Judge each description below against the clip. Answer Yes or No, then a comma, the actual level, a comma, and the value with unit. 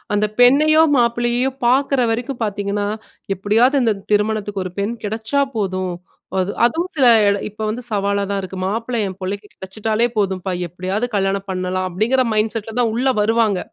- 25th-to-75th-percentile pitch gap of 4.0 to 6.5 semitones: No, average, 3.5 semitones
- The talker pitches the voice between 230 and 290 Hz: No, high, 215 Hz